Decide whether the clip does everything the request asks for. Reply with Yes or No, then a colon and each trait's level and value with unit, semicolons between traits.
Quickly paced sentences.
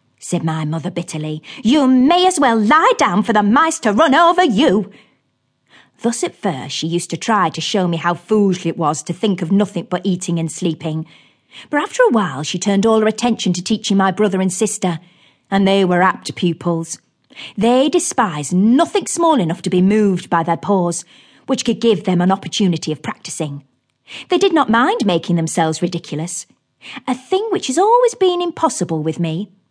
No: average, 190 wpm